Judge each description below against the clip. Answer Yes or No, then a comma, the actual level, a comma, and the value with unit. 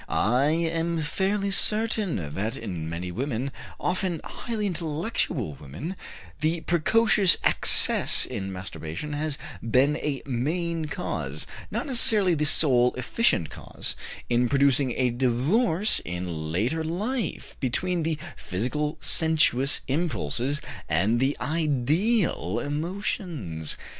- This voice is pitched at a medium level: Yes, medium, 150 Hz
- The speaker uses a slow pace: Yes, slow, 110 wpm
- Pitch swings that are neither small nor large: No, wide, 6.3 semitones